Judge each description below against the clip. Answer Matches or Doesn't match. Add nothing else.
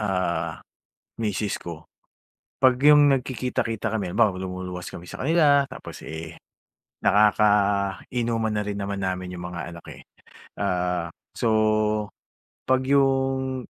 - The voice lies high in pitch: Doesn't match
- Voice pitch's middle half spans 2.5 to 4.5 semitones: Doesn't match